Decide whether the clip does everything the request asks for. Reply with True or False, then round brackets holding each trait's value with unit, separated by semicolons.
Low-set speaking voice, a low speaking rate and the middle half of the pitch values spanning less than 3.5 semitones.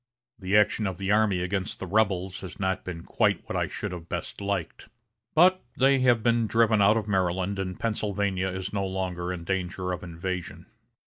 False (95 Hz; 190 wpm; 2.4 semitones)